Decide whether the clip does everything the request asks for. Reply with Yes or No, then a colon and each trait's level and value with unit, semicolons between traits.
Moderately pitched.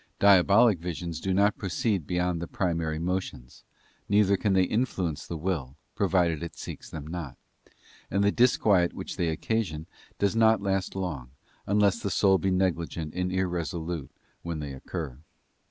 No: very low, 90 Hz